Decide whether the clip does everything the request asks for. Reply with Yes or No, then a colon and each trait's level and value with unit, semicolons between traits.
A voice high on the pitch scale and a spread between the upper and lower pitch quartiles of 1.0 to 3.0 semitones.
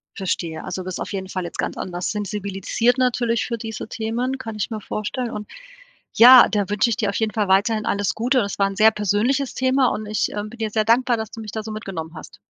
Yes: high, 215 Hz; average, 2.7 semitones